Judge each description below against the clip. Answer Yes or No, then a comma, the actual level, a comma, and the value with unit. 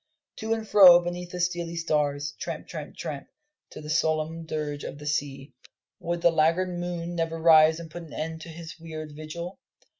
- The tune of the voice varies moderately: No, narrow, 1.9 semitones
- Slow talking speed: No, average, 185 wpm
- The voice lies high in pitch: No, medium, 165 Hz